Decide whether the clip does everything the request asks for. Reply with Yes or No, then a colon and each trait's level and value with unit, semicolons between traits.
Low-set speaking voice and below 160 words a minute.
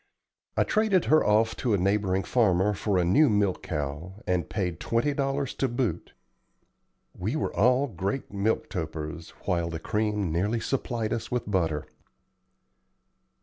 Yes: low, 105 Hz; average, 145 wpm